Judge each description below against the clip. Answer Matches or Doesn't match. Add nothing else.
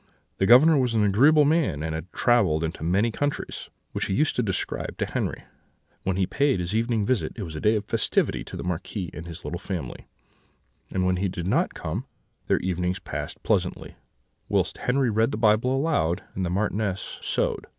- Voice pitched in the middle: Doesn't match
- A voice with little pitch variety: Doesn't match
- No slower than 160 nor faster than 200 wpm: Matches